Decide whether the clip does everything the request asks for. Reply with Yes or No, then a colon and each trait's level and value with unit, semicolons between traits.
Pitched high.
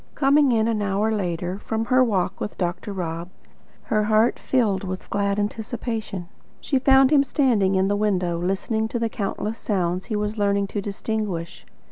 Yes: high, 210 Hz